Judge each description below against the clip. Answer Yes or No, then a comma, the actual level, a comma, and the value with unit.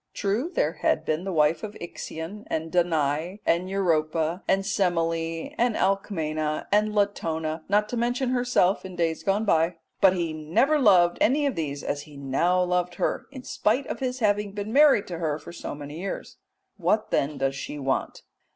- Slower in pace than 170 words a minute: No, average, 180 wpm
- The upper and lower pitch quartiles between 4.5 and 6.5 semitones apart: Yes, average, 4.8 semitones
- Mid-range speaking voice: Yes, medium, 180 Hz